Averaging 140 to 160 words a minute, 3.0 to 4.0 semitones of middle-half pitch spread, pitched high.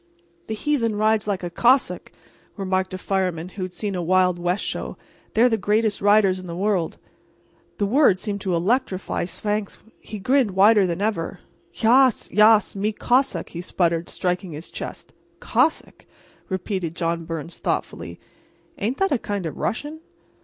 Yes: average, 155 wpm; average, 3.3 semitones; high, 200 Hz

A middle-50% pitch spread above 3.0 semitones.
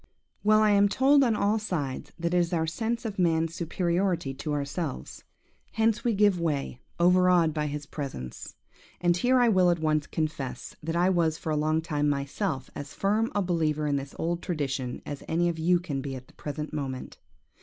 Yes: average, 4.1 semitones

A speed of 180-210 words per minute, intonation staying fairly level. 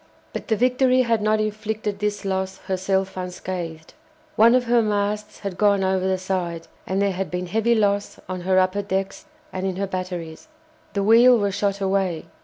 Yes: average, 185 wpm; narrow, 2.3 semitones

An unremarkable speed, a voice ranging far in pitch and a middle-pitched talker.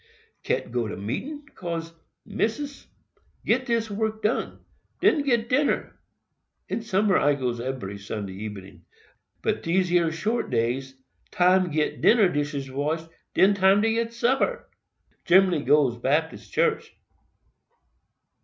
No: slow, 125 wpm; wide, 8.9 semitones; medium, 180 Hz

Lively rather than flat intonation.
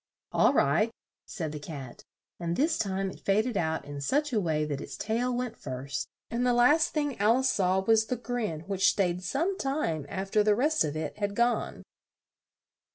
Yes: wide, 7.1 semitones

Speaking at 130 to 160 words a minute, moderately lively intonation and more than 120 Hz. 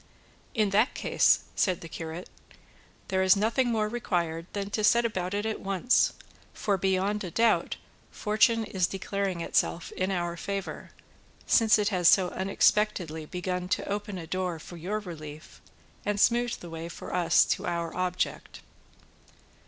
Yes: average, 155 wpm; average, 3.3 semitones; high, 190 Hz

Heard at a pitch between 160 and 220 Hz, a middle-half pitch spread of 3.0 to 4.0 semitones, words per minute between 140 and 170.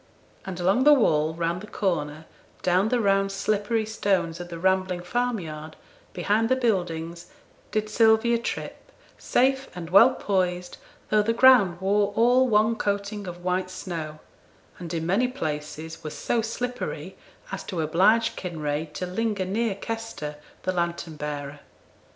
No: high, 190 Hz; average, 4.7 semitones; average, 150 wpm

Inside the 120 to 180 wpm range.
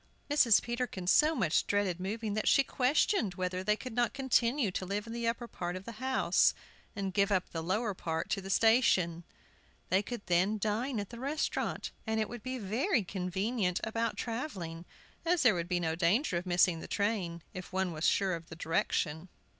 No: average, 195 wpm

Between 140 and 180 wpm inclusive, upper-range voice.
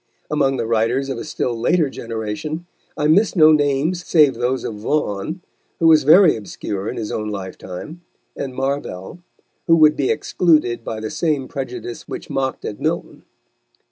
No: average, 165 wpm; low, 135 Hz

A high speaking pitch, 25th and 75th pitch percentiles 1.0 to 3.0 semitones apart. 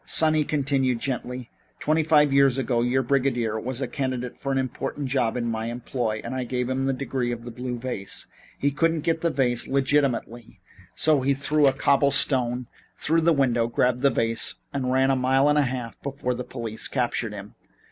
No: low, 130 Hz; narrow, 2.5 semitones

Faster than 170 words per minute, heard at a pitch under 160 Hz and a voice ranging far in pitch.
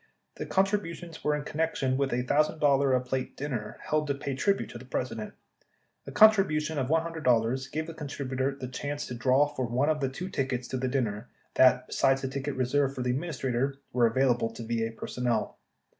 No: average, 200 wpm; low, 135 Hz; average, 3.0 semitones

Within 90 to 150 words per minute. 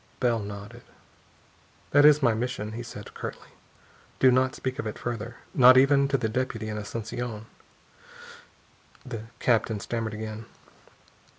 Yes: slow, 135 wpm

